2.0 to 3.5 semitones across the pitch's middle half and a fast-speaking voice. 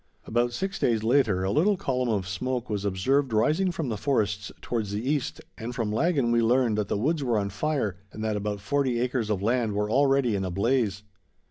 No: average, 4.5 semitones; fast, 215 wpm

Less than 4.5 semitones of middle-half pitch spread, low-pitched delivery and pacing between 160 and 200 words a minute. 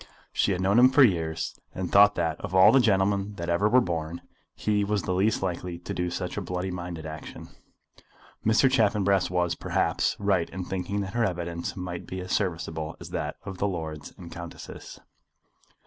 Yes: average, 2.9 semitones; very low, 90 Hz; average, 190 wpm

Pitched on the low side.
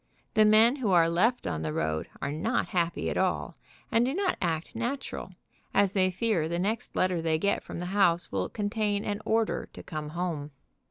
No: medium, 185 Hz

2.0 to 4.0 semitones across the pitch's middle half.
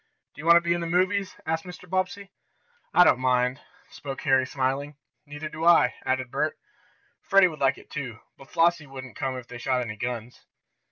No: average, 4.8 semitones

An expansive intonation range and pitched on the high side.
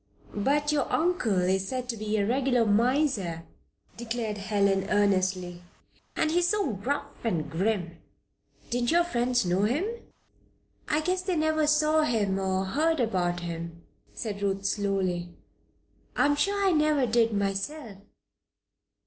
Yes: wide, 7.4 semitones; high, 225 Hz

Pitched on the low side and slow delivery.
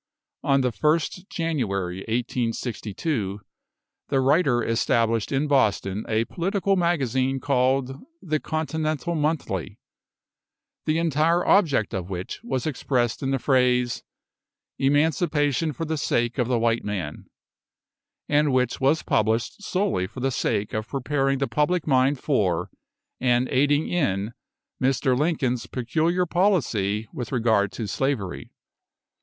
Yes: low, 130 Hz; slow, 125 wpm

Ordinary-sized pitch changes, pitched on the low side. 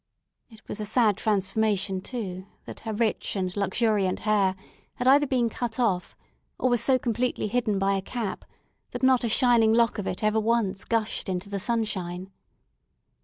No: average, 3.3 semitones; high, 215 Hz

